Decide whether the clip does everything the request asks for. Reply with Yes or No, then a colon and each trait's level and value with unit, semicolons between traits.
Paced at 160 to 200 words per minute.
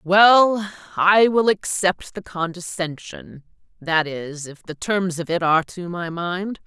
No: average, 145 wpm